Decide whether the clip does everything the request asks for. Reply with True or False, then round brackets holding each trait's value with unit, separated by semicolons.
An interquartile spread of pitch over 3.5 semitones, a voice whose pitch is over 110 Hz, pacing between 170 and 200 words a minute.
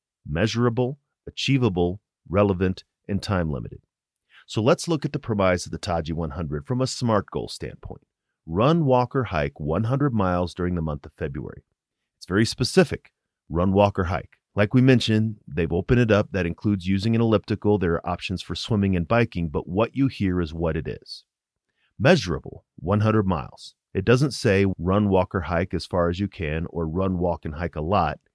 False (4.6 semitones; 95 Hz; 185 wpm)